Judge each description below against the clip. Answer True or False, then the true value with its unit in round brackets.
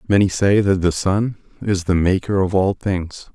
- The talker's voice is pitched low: True (95 Hz)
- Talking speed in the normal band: True (195 wpm)